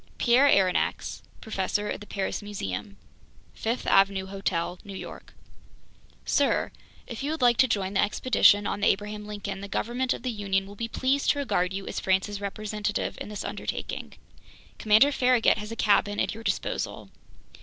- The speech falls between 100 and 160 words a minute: No, average, 170 wpm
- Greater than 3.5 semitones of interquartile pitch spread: No, average, 2.8 semitones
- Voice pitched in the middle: No, high, 210 Hz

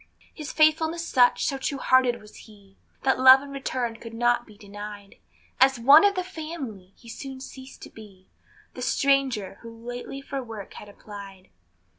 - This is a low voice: No, high, 245 Hz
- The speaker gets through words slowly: No, average, 170 wpm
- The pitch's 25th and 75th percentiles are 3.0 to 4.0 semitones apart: No, average, 4.5 semitones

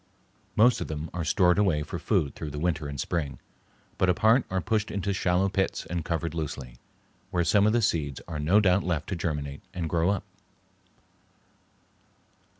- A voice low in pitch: Yes, very low, 85 Hz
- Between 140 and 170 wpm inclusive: No, average, 180 wpm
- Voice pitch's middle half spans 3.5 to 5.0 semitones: Yes, average, 4.3 semitones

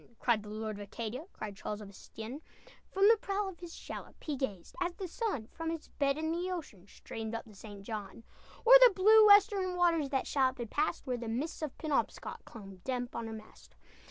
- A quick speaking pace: Yes, fast, 215 wpm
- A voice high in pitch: Yes, very high, 265 Hz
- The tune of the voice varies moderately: No, wide, 8.2 semitones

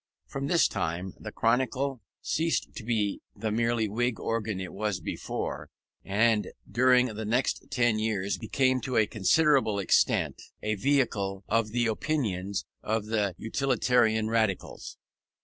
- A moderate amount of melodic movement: Yes, average, 3.3 semitones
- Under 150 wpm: Yes, slow, 135 wpm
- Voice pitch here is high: No, low, 110 Hz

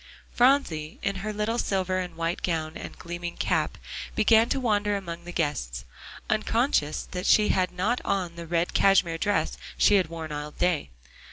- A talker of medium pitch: Yes, medium, 180 Hz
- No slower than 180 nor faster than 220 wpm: No, average, 170 wpm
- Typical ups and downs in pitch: Yes, average, 3.9 semitones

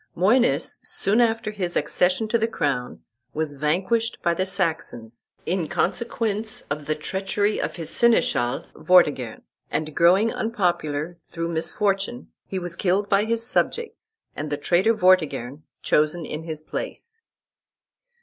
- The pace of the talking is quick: No, slow, 135 wpm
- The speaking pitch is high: No, medium, 180 Hz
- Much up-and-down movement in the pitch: Yes, wide, 5.8 semitones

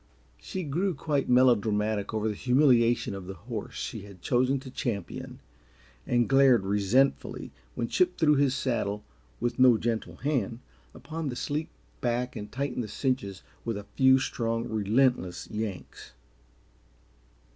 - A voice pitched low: Yes, low, 120 Hz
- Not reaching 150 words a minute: Yes, average, 140 wpm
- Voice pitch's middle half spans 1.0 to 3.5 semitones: No, average, 4.3 semitones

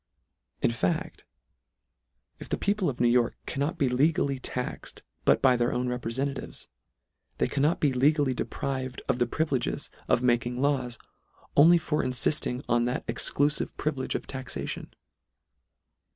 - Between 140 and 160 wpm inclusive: Yes, average, 145 wpm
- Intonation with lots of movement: No, average, 2.8 semitones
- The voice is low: Yes, low, 130 Hz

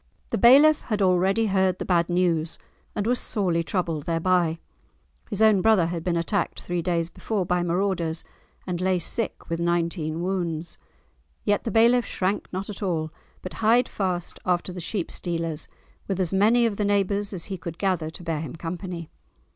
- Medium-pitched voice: Yes, medium, 180 Hz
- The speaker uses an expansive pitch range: No, average, 3.2 semitones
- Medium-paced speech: Yes, average, 180 wpm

